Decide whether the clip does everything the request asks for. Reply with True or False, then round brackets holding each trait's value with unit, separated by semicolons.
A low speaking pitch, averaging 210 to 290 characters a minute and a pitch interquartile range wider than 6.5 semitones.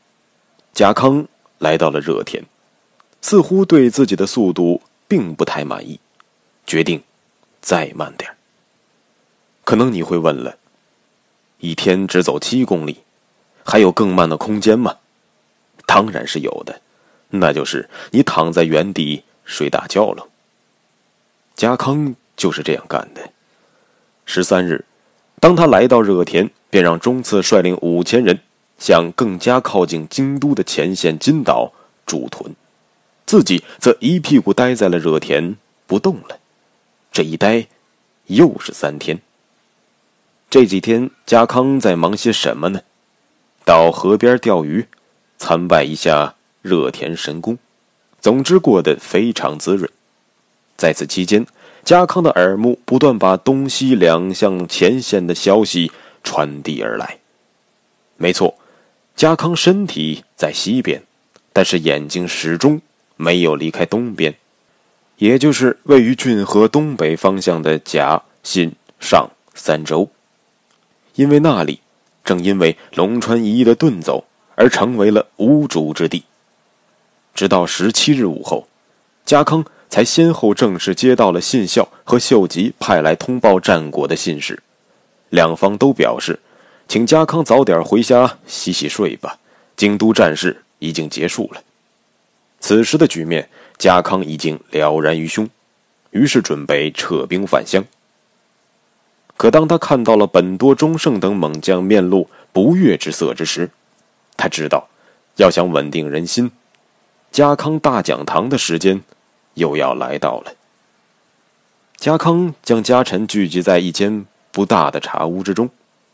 False (105 Hz; 195 characters per minute; 7.3 semitones)